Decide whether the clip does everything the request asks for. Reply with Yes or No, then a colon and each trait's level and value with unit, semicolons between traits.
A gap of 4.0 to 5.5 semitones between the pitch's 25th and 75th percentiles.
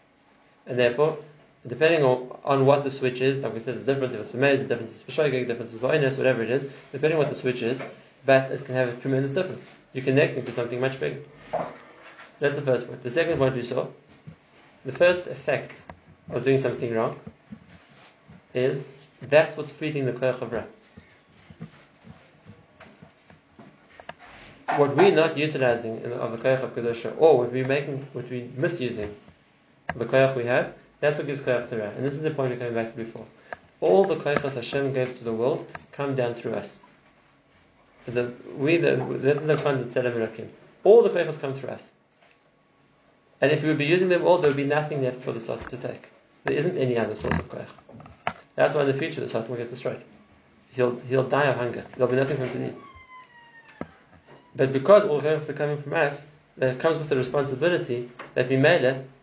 No: average, 3.0 semitones